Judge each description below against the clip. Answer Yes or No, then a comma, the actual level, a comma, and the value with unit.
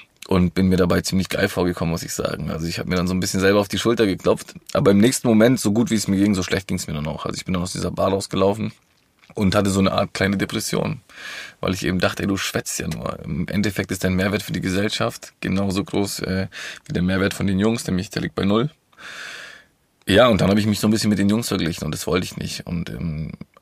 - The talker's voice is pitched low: Yes, very low, 95 Hz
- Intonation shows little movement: Yes, narrow, 2.1 semitones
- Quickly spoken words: Yes, fast, 270 wpm